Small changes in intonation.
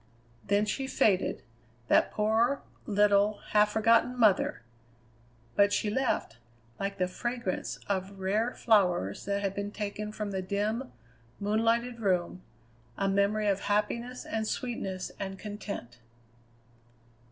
Yes: narrow, 2.1 semitones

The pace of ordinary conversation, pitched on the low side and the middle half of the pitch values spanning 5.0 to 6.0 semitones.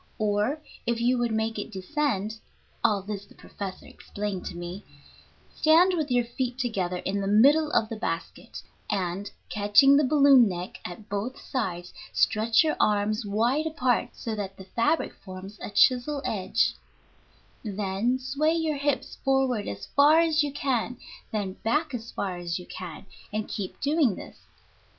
No: average, 160 wpm; high, 225 Hz; average, 5.3 semitones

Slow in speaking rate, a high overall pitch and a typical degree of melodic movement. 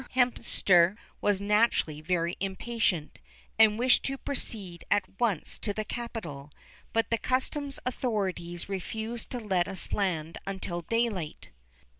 Yes: slow, 125 wpm; high, 205 Hz; average, 4.9 semitones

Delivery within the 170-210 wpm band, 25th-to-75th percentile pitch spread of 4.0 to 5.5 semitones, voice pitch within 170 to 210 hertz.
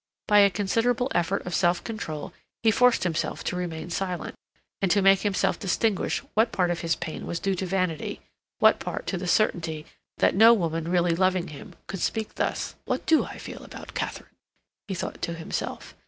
No: average, 190 wpm; average, 3.3 semitones; medium, 185 Hz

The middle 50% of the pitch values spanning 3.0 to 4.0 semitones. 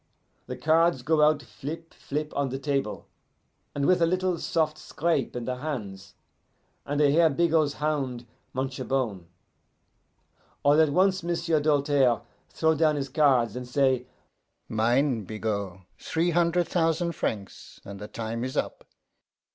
No: average, 4.4 semitones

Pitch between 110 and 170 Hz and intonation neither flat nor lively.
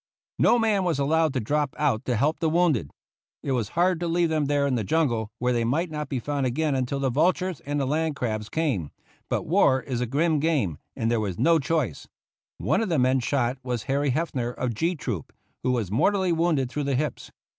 Yes: medium, 140 Hz; average, 4.7 semitones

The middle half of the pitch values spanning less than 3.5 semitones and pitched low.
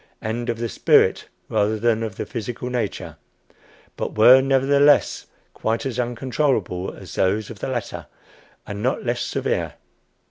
Yes: average, 2.9 semitones; low, 120 Hz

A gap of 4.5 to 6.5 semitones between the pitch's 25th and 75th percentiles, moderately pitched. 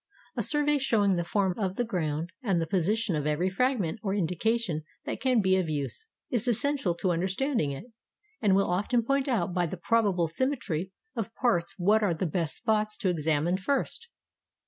No: average, 5.1 semitones; high, 195 Hz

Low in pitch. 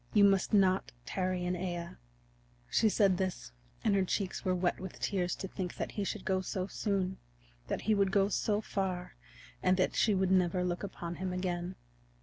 No: medium, 185 Hz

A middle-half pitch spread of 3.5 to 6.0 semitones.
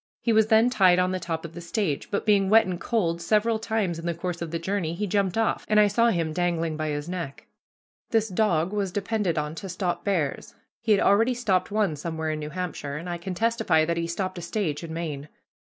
Yes: average, 4.0 semitones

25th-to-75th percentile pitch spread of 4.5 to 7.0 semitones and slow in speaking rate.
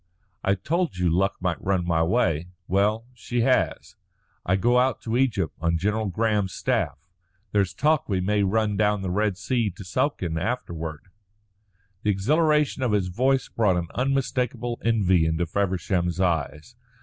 No: average, 5.2 semitones; average, 155 wpm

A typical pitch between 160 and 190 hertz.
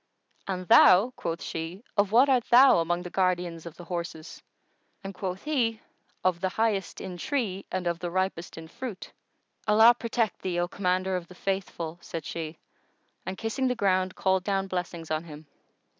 Yes: medium, 185 Hz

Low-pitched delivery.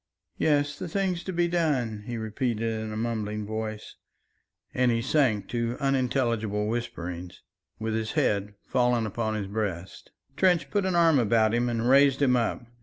Yes: low, 115 Hz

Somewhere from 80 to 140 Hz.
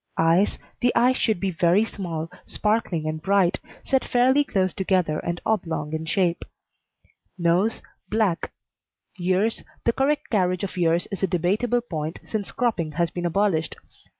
No: medium, 185 Hz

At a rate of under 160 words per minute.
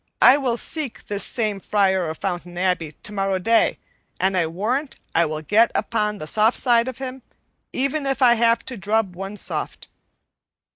No: average, 175 wpm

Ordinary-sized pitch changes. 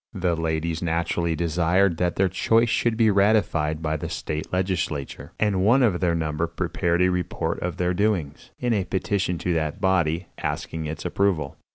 Yes: average, 3.0 semitones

